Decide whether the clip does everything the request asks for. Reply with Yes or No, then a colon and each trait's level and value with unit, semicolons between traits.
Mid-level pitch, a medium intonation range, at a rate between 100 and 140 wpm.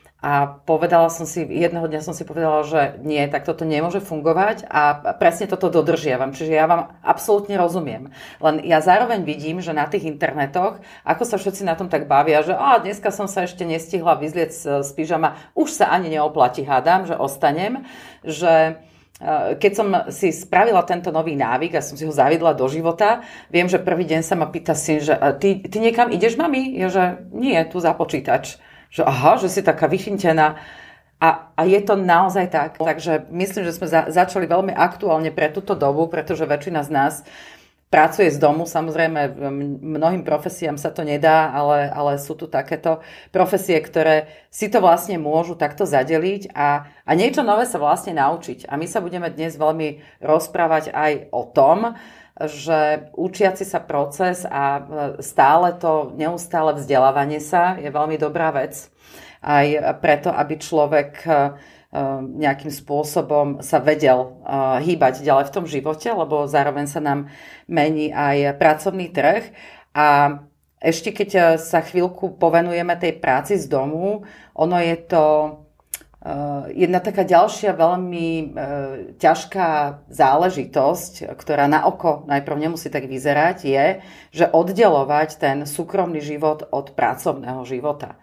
No: medium, 160 Hz; average, 3.3 semitones; average, 155 wpm